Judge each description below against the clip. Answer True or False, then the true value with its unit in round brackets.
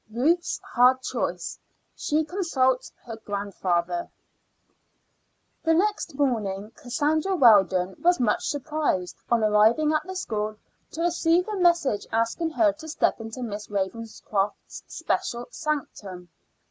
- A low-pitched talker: False (245 Hz)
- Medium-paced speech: False (120 wpm)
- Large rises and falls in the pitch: True (7.1 semitones)